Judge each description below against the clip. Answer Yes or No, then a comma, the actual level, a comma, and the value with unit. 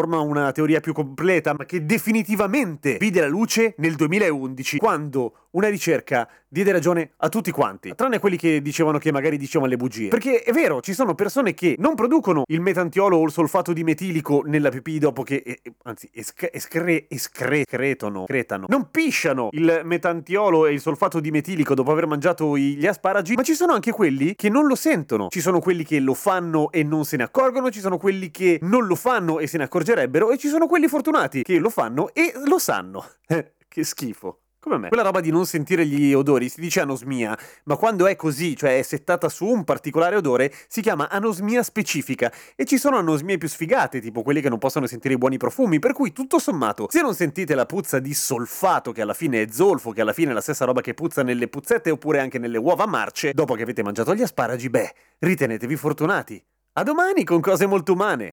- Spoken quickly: Yes, fast, 210 wpm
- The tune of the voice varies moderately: No, wide, 6.1 semitones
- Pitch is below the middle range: No, medium, 165 Hz